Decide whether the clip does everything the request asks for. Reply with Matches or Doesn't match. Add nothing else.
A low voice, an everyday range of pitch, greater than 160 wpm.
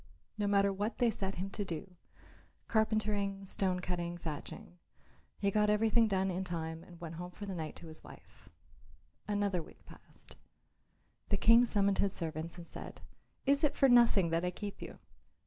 Doesn't match